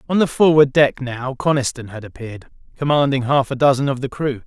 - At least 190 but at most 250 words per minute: Yes, average, 200 wpm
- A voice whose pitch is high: No, low, 135 Hz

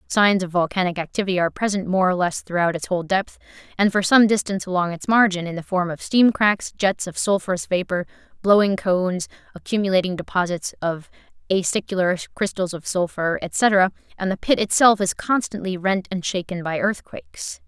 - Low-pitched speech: No, high, 190 Hz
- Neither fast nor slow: Yes, average, 175 wpm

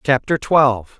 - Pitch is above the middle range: No, low, 130 Hz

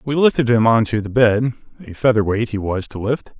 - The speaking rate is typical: No, fast, 210 wpm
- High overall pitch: No, low, 115 Hz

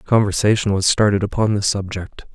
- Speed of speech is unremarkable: Yes, average, 155 wpm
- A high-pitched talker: No, low, 100 Hz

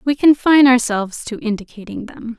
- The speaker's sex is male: No, female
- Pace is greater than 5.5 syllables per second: Yes, 5.7 syllables/s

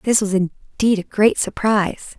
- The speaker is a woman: Yes, female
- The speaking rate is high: No, average, 165 wpm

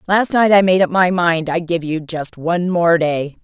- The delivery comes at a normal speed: No, fast, 245 wpm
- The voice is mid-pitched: Yes, medium, 175 Hz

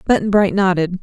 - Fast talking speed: No, average, 175 wpm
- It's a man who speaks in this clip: No, female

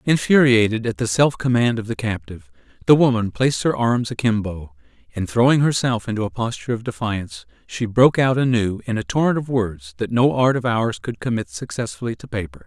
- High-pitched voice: No, low, 115 Hz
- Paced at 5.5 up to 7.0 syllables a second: Yes, 5.7 syllables/s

